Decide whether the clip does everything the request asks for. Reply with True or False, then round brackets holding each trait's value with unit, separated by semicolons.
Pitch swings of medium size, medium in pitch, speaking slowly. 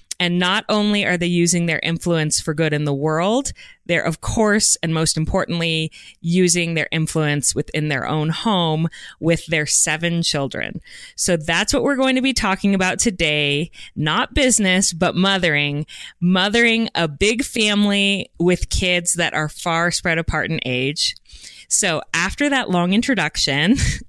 False (4.0 semitones; 170 Hz; 155 wpm)